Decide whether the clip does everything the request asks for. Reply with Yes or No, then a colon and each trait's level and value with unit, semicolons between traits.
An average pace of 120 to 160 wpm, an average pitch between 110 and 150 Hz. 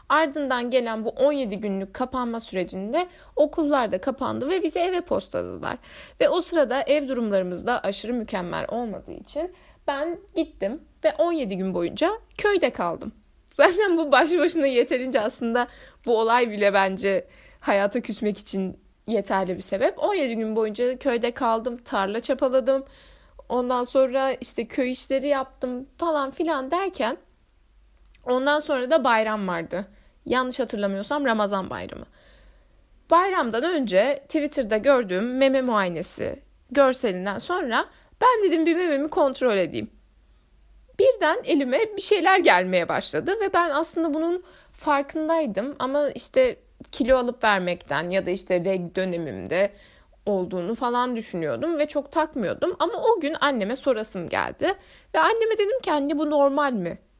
No: average, 135 wpm; very high, 265 Hz